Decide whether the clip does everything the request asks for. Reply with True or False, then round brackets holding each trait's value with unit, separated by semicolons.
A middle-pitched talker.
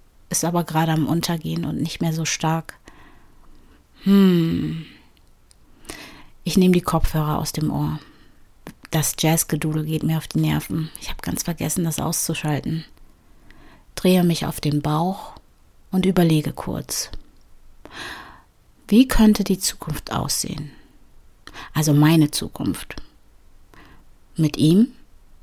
True (160 Hz)